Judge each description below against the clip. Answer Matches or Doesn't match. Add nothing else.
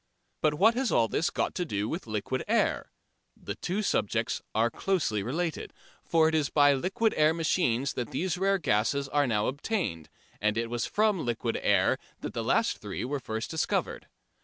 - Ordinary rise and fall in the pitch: Doesn't match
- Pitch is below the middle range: Doesn't match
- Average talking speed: Matches